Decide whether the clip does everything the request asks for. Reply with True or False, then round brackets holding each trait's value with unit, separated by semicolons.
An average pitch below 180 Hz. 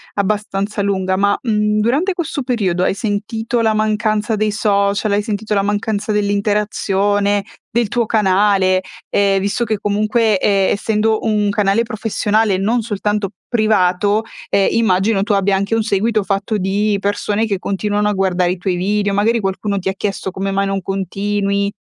False (205 Hz)